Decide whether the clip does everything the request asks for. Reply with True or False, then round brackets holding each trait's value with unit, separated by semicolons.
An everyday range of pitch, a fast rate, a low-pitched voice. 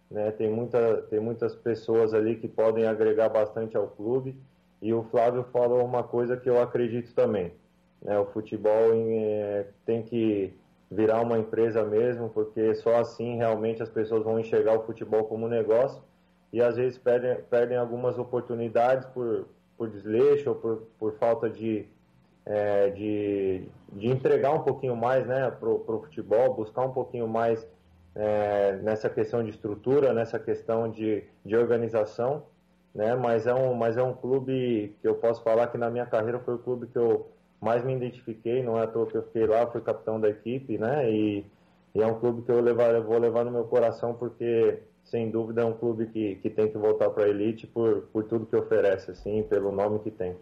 False (1.8 semitones; 195 wpm; 115 Hz)